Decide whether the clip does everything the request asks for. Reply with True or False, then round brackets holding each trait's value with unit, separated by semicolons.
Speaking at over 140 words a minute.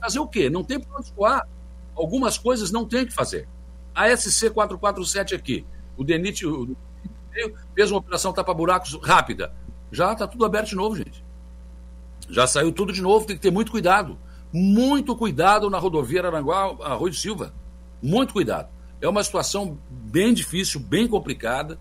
True (160 wpm)